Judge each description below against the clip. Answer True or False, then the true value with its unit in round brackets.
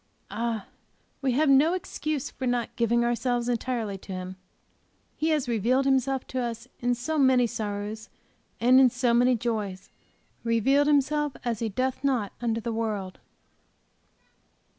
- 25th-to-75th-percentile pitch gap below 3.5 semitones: True (2.7 semitones)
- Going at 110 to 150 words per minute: True (145 wpm)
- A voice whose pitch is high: True (240 Hz)